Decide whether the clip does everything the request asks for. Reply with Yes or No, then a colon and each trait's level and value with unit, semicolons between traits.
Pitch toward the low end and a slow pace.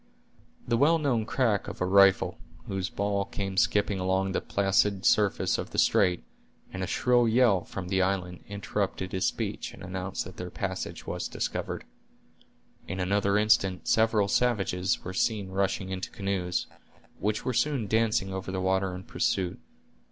No: very low, 95 Hz; average, 160 wpm